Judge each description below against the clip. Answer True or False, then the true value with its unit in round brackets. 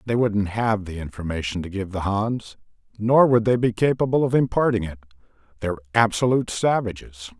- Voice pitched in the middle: False (105 Hz)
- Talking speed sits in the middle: True (160 wpm)